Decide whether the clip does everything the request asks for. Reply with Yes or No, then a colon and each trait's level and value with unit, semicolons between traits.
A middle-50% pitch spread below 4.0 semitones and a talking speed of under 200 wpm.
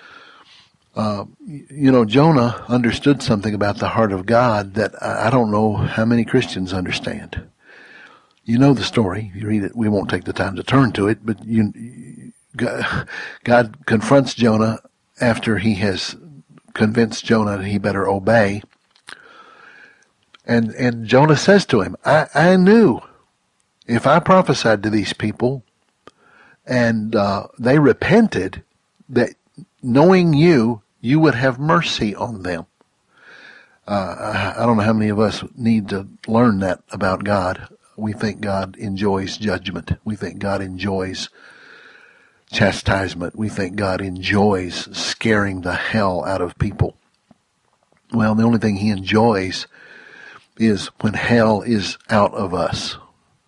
Yes: average, 3.3 semitones; average, 140 wpm